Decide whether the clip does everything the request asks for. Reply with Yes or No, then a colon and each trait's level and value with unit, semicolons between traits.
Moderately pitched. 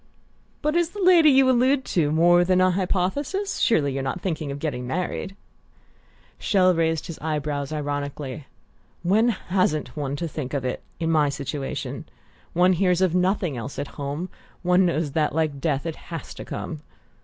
Yes: medium, 165 Hz